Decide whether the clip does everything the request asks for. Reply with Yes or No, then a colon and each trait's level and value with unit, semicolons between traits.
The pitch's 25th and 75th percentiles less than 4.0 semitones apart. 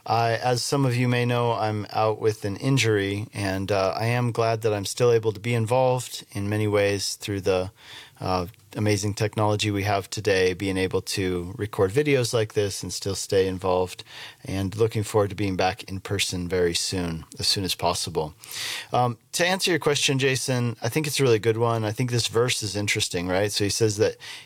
Yes: average, 3.5 semitones